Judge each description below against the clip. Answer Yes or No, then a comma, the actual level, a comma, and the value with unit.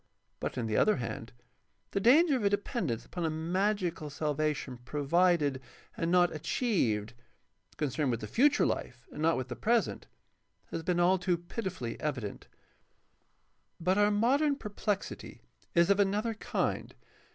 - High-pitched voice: No, medium, 175 Hz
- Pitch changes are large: Yes, wide, 5.9 semitones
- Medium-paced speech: Yes, average, 150 wpm